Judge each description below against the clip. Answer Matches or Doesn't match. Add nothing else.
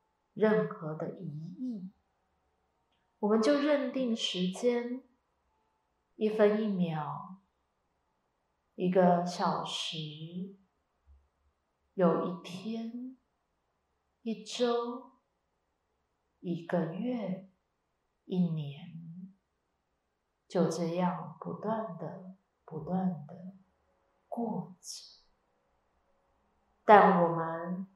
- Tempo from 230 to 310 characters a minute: Doesn't match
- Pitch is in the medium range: Matches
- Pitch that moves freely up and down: Doesn't match